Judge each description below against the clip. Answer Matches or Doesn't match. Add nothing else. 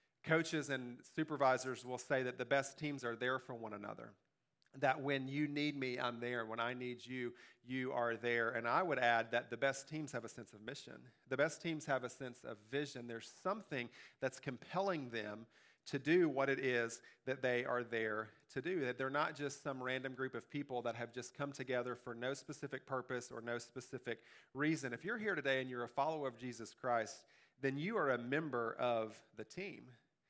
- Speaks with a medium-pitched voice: Doesn't match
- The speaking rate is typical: Doesn't match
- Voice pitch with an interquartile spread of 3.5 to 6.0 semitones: Doesn't match